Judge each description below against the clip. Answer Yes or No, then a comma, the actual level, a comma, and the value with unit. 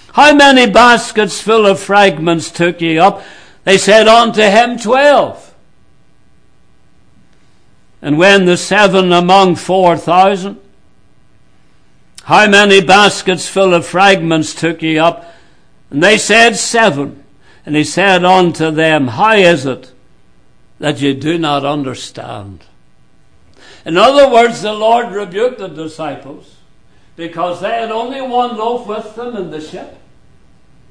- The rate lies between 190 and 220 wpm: No, slow, 130 wpm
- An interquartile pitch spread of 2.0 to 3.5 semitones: No, average, 5.3 semitones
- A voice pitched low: No, high, 190 Hz